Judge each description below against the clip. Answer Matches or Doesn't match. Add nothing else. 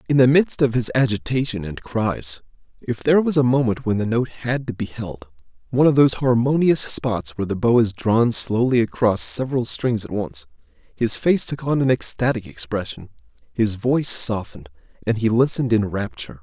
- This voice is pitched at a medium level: Doesn't match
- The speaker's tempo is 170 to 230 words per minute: Matches